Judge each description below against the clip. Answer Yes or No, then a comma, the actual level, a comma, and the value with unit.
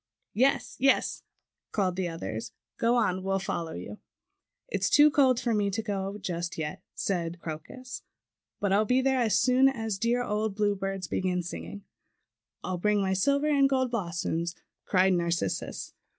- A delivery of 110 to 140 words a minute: No, average, 155 wpm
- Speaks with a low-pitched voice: No, high, 195 Hz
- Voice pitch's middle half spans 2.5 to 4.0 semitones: No, wide, 5.5 semitones